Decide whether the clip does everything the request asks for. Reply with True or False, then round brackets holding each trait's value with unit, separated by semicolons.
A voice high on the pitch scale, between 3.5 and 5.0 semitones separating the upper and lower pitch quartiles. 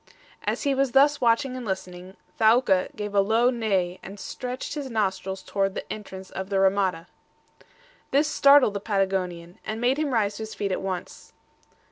True (205 Hz; 4.6 semitones)